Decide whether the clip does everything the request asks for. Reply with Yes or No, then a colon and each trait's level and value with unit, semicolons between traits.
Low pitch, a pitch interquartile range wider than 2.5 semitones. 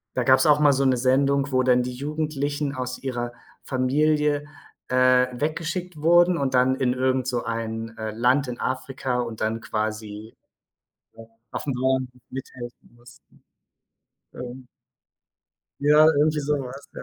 Yes: low, 130 Hz; average, 2.9 semitones